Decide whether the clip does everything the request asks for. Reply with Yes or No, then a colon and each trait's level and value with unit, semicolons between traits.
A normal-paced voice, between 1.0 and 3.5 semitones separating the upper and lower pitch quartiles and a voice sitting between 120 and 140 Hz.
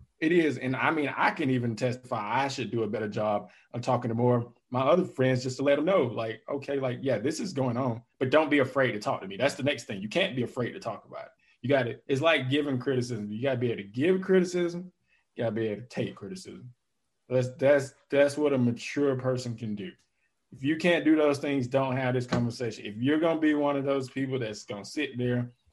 No: fast, 250 wpm; average, 2.9 semitones; low, 130 Hz